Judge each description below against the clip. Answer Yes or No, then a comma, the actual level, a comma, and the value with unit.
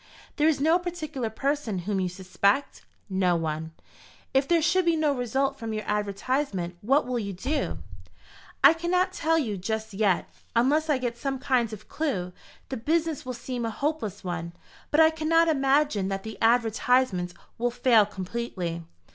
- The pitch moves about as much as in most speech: No, wide, 6.8 semitones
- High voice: Yes, high, 245 Hz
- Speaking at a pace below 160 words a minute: No, average, 165 wpm